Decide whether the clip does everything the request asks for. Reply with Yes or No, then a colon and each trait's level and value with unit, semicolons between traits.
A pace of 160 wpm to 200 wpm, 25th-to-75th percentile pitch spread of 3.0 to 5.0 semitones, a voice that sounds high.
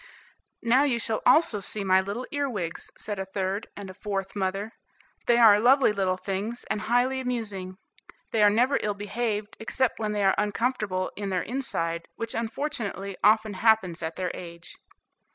Yes: average, 170 wpm; average, 3.5 semitones; high, 210 Hz